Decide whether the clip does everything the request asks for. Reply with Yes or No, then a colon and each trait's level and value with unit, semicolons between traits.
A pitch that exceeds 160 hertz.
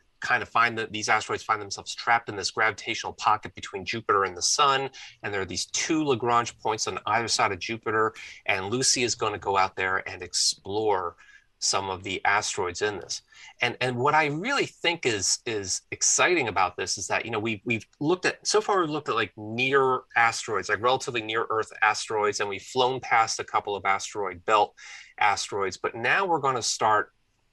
No: medium, 140 Hz